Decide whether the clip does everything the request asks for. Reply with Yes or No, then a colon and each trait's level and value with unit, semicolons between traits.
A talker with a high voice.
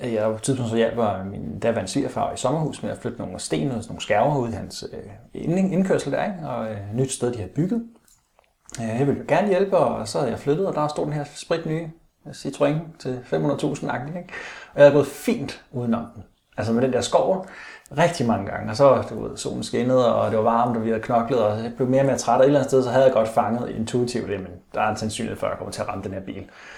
No: low, 125 Hz